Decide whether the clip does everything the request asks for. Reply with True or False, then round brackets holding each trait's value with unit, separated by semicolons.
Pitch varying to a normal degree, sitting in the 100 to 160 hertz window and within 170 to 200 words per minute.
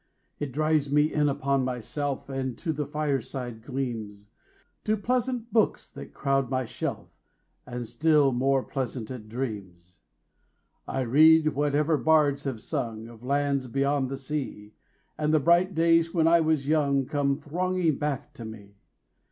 False (3.5 semitones; 140 Hz; 150 wpm)